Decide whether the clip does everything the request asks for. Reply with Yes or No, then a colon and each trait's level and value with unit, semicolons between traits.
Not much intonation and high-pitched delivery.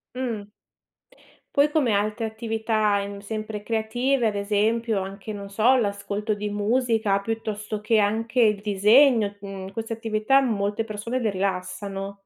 Yes: narrow, 2.0 semitones; high, 215 Hz